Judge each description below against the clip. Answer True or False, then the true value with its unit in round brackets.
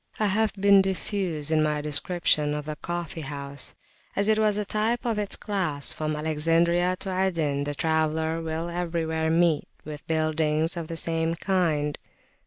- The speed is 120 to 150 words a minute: False (165 wpm)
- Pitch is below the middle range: False (165 Hz)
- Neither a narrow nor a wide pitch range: True (3.4 semitones)